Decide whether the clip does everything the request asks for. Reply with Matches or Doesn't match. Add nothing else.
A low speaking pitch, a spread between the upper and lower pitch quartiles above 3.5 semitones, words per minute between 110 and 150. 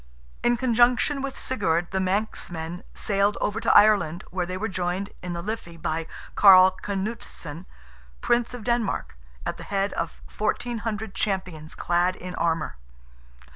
Doesn't match